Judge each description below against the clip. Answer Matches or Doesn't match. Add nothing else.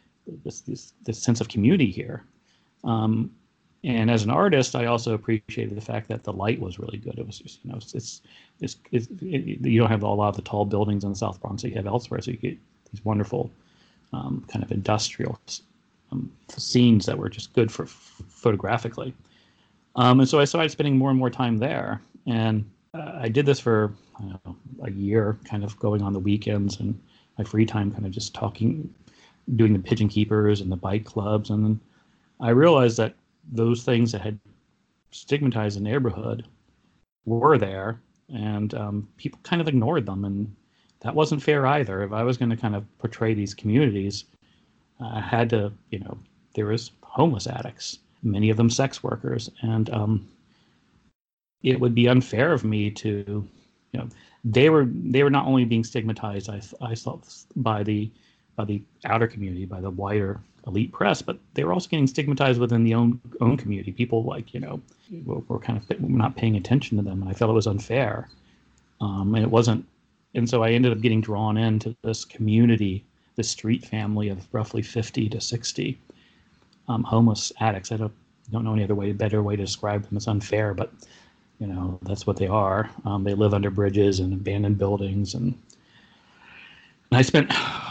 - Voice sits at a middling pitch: Doesn't match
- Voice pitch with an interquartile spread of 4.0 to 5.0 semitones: Doesn't match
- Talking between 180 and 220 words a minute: Matches